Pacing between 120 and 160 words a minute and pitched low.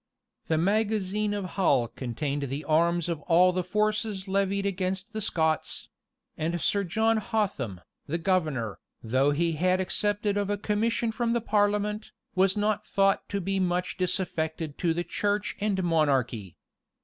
No: average, 155 wpm; medium, 185 Hz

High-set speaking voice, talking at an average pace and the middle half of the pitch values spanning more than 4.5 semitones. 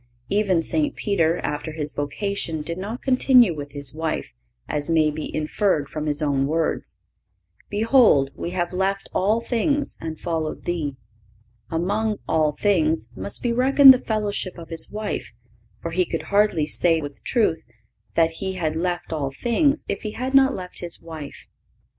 No: medium, 175 Hz; average, 165 wpm; wide, 5.4 semitones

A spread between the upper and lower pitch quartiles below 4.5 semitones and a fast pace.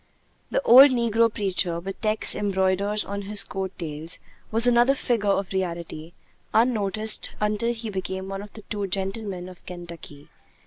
No: average, 2.9 semitones; average, 150 wpm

